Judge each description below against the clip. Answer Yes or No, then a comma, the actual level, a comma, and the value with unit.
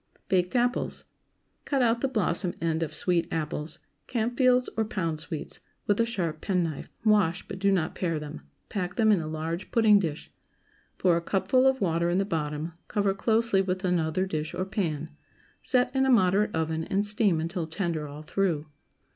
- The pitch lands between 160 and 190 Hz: Yes, medium, 185 Hz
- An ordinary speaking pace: Yes, average, 175 wpm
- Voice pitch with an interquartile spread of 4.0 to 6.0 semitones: Yes, average, 4.6 semitones